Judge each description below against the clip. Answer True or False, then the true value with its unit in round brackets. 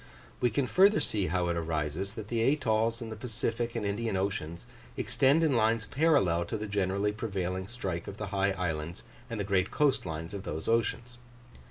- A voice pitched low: True (105 Hz)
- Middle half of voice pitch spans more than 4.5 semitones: False (4.0 semitones)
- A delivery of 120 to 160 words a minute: False (185 wpm)